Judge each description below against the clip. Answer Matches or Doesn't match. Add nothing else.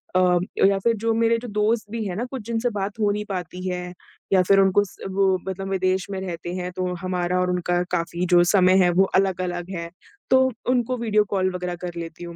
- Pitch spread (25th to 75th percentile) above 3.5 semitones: Doesn't match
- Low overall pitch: Doesn't match